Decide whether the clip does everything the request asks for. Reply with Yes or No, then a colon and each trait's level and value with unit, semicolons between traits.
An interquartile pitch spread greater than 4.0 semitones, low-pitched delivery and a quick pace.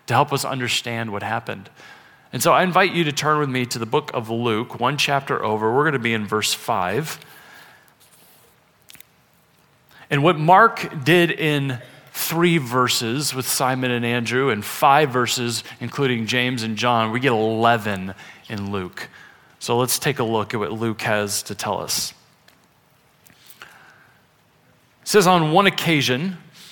No: average, 4.9 semitones; low, 125 Hz; average, 155 wpm